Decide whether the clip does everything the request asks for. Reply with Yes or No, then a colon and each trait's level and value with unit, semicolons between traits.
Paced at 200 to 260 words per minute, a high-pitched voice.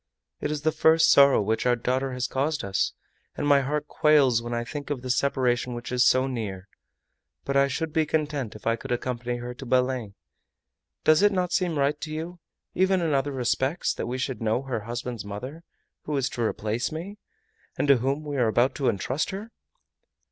No: fast, 205 wpm; low, 135 Hz